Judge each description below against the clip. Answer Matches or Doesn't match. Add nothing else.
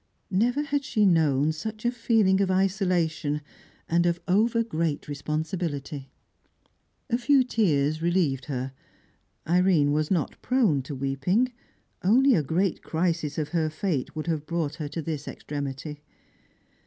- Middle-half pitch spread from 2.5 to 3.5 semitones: Doesn't match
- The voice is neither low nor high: Matches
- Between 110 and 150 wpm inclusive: Matches